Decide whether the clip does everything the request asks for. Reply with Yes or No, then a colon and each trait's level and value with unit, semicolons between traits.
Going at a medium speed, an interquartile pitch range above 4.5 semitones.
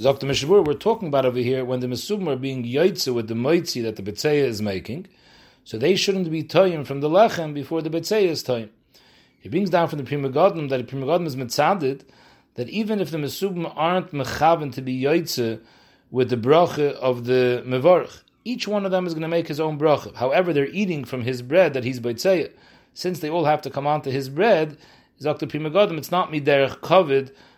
No: fast, 210 wpm; average, 5.2 semitones